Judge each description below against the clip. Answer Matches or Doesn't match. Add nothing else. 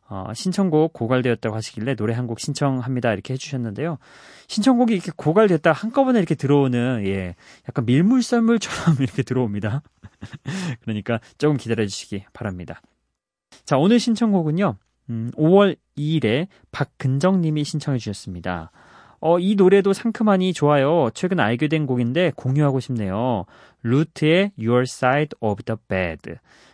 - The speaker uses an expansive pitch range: Matches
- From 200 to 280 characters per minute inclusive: Doesn't match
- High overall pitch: Doesn't match